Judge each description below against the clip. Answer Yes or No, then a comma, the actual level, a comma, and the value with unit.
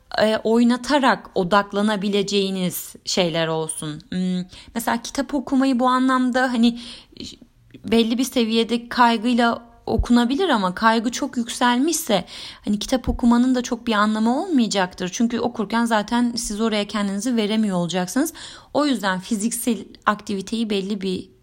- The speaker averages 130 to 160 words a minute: No, average, 115 wpm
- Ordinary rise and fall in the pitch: Yes, average, 3.3 semitones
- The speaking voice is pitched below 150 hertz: No, high, 230 Hz